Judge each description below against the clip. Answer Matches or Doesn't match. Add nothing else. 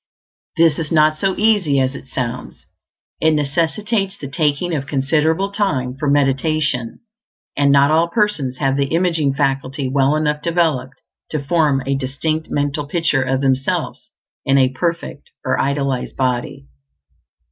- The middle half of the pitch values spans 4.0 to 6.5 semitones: Doesn't match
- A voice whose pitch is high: Doesn't match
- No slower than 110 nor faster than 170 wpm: Matches